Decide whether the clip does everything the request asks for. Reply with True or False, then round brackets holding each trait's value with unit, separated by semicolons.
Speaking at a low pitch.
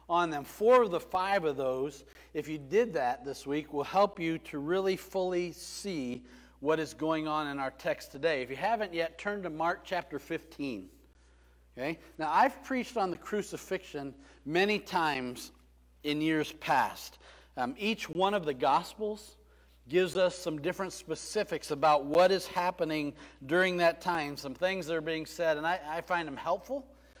False (165 Hz)